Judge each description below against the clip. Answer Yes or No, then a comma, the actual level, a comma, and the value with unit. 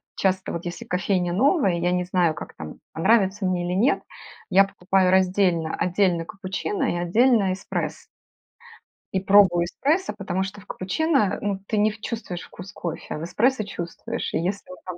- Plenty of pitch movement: No, narrow, 2.6 semitones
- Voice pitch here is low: No, high, 190 Hz